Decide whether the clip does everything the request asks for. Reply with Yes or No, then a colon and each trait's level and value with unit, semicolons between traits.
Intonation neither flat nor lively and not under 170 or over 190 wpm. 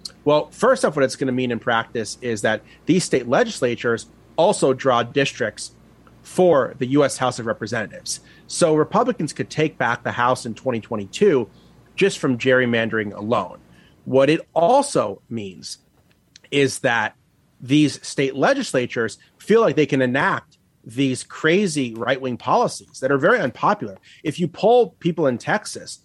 No: average, 4.1 semitones; average, 150 wpm